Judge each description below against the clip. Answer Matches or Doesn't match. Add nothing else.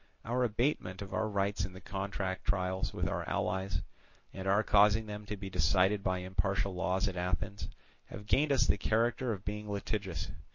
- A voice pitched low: Matches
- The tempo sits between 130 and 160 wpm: Doesn't match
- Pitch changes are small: Matches